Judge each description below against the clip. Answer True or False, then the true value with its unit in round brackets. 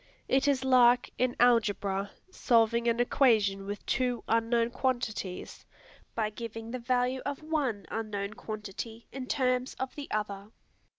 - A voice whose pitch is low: False (235 Hz)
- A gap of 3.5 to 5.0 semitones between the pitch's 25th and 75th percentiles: False (3.0 semitones)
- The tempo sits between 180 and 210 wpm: False (135 wpm)